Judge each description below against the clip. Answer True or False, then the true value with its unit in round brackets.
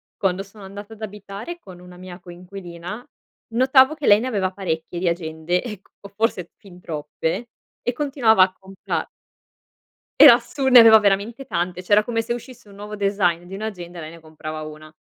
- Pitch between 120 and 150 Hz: False (195 Hz)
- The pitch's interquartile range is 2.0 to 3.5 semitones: False (3.9 semitones)